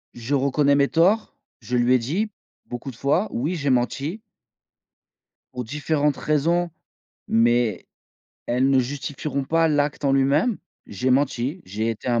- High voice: No, medium, 140 Hz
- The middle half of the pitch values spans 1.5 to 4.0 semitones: Yes, average, 3.6 semitones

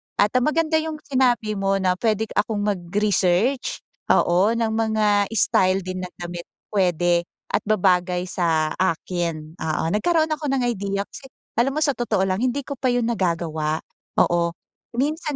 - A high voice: Yes, high, 205 Hz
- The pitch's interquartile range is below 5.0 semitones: No, wide, 5.6 semitones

